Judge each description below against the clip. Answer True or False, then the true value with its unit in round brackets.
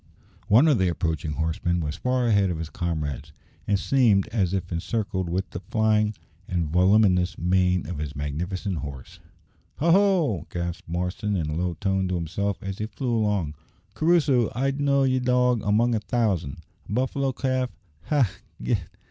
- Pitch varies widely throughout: True (5.9 semitones)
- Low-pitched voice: True (95 Hz)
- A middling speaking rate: True (165 wpm)